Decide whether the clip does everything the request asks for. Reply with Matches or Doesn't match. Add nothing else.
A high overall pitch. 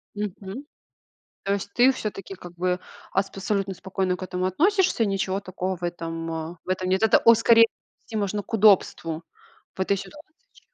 Matches